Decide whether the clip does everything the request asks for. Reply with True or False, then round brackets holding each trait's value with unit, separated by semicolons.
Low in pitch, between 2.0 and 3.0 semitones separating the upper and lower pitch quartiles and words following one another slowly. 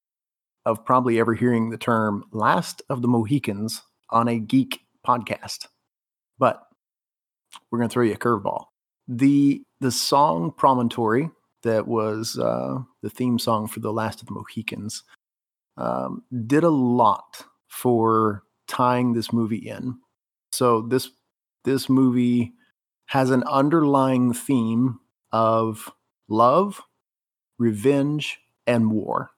True (120 Hz; 2.4 semitones; 125 wpm)